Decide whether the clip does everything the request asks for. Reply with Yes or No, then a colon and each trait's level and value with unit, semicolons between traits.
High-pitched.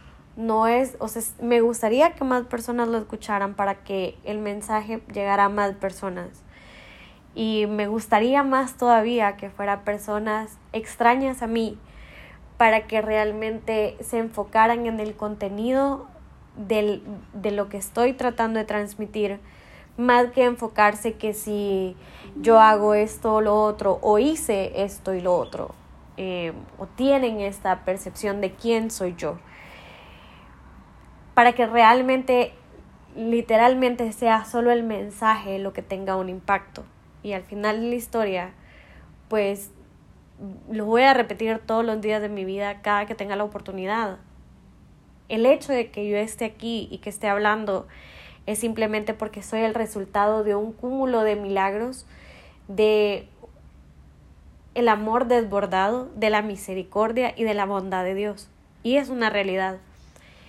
Yes: high, 215 Hz